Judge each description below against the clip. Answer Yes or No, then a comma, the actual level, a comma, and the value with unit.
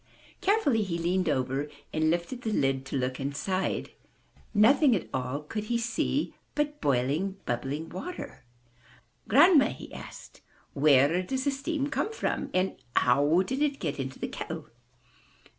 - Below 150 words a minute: Yes, average, 140 wpm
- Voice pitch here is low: No, medium, 180 Hz